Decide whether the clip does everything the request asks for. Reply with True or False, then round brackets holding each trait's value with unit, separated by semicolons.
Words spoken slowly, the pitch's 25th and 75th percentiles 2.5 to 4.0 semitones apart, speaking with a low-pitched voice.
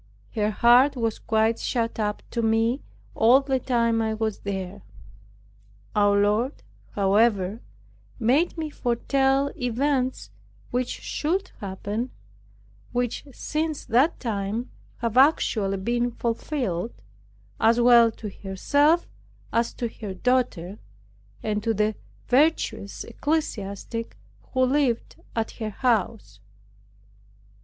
False (110 wpm; 3.6 semitones; 230 Hz)